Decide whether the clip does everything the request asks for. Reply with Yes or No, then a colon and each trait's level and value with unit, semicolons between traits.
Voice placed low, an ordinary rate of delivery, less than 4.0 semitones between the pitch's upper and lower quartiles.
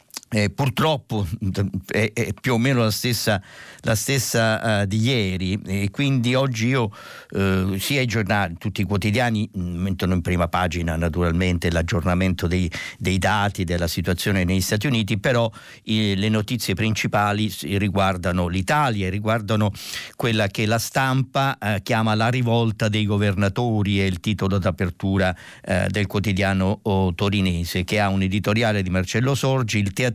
Yes: low, 105 Hz; average, 150 wpm; average, 3.1 semitones